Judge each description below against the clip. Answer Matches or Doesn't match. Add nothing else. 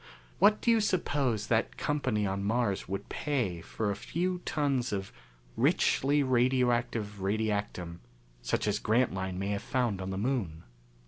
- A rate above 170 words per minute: Doesn't match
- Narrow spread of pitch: Doesn't match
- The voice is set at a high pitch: Doesn't match